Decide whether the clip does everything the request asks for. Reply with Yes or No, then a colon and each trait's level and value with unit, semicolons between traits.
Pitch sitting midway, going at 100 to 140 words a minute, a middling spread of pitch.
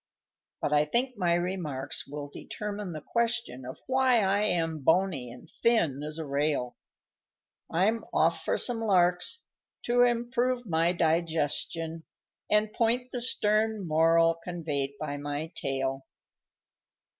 No: medium, 170 Hz; slow, 135 wpm; wide, 6.6 semitones